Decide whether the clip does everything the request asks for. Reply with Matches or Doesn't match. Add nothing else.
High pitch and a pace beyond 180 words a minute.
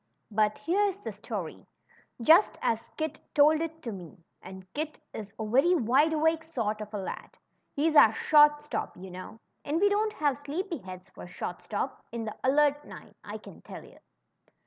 Matches